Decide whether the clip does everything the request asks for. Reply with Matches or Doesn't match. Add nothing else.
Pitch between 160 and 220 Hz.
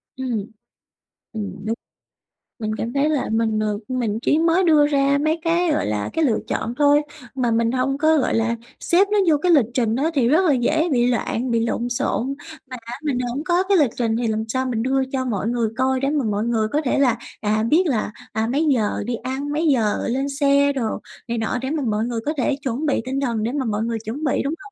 Doesn't match